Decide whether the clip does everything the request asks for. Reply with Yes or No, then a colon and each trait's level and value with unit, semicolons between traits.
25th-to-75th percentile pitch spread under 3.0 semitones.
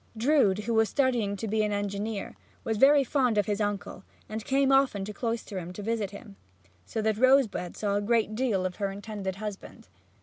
Yes: narrow, 2.6 semitones